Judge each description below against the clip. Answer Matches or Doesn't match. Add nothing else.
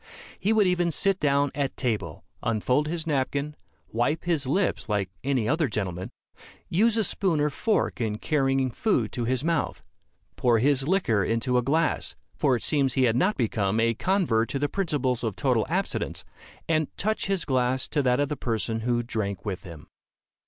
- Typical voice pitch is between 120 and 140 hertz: Matches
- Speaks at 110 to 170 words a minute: Doesn't match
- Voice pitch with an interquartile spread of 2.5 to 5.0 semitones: Doesn't match